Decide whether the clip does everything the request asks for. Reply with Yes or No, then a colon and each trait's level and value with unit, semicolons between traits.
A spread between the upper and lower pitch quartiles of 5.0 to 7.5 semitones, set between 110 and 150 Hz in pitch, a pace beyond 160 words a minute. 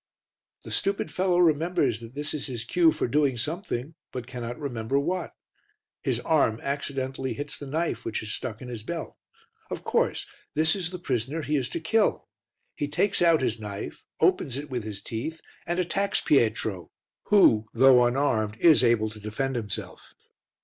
Yes: wide, 5.5 semitones; low, 135 Hz; average, 170 wpm